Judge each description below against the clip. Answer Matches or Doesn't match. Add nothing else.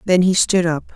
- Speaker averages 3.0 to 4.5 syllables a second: Doesn't match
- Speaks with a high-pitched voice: Doesn't match